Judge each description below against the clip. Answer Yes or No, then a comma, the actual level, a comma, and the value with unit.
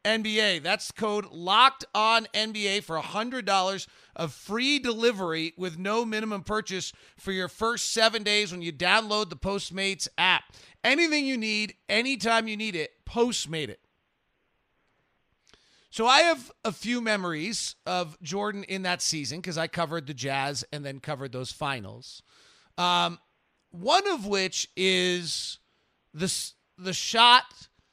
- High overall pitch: Yes, high, 195 Hz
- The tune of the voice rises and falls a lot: No, average, 4.5 semitones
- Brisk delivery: No, average, 140 wpm